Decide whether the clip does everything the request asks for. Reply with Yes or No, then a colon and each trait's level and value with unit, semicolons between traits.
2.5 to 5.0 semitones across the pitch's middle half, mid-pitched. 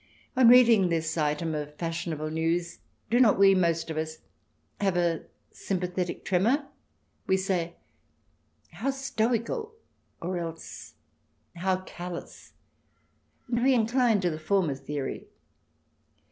No: wide, 5.4 semitones; medium, 180 Hz